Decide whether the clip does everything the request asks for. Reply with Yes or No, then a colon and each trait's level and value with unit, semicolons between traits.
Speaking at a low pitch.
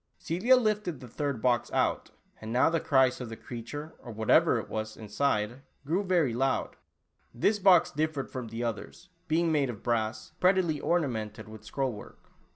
Yes: low, 130 Hz